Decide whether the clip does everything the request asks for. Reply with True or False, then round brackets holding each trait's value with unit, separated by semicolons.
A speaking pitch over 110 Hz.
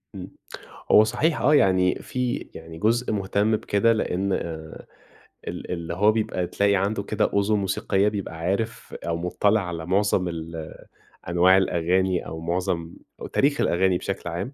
False (95 Hz)